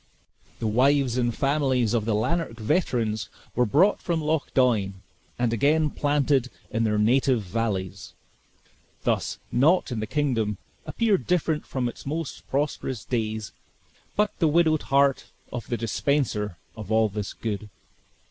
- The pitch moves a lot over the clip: No, average, 5.0 semitones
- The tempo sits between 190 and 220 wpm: No, average, 140 wpm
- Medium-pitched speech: No, low, 125 Hz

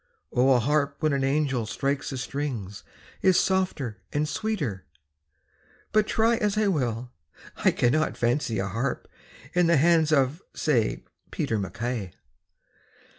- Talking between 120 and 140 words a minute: Yes, slow, 135 wpm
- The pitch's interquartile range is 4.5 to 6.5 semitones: Yes, average, 5.1 semitones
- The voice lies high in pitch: No, medium, 140 Hz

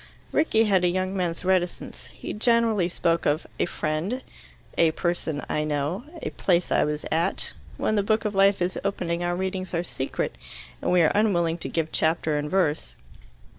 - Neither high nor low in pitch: Yes, medium, 175 Hz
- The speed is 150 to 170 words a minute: No, average, 180 wpm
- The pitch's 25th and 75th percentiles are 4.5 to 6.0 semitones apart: No, average, 3.2 semitones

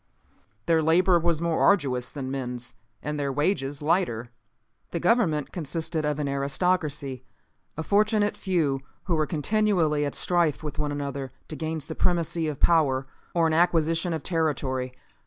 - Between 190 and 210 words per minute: No, average, 150 wpm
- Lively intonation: No, average, 3.5 semitones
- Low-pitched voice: No, medium, 155 Hz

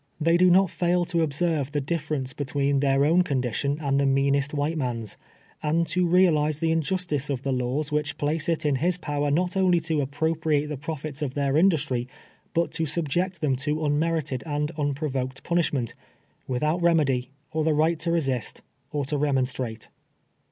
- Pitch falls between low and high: Yes, medium, 150 Hz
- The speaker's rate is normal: Yes, average, 180 wpm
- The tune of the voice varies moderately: Yes, average, 3.1 semitones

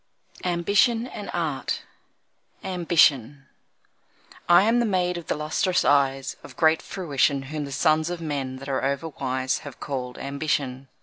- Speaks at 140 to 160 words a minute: Yes, average, 145 wpm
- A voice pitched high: No, medium, 150 Hz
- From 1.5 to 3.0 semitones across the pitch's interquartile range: No, average, 4.3 semitones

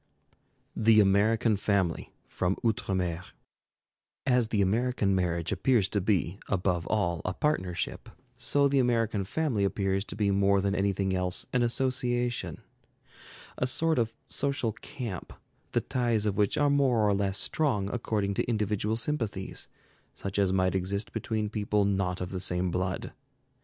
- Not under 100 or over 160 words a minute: Yes, average, 150 wpm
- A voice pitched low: Yes, low, 105 Hz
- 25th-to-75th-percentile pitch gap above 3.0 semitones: Yes, average, 3.7 semitones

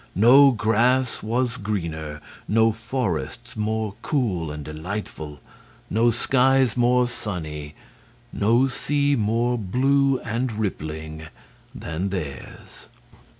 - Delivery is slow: Yes, slow, 100 wpm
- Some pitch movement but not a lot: No, wide, 6.9 semitones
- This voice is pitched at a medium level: No, low, 110 Hz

